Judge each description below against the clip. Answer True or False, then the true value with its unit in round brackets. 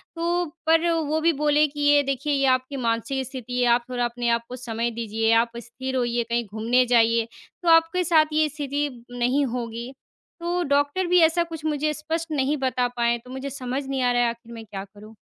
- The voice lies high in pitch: True (260 Hz)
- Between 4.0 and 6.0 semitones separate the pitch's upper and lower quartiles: True (4.3 semitones)